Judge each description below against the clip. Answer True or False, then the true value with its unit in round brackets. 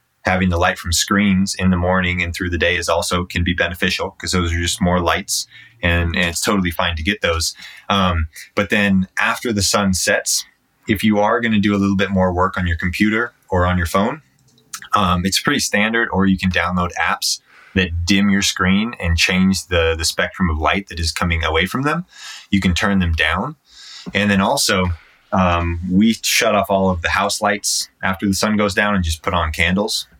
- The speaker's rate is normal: False (215 wpm)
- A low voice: True (95 Hz)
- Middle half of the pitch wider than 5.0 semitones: False (2.5 semitones)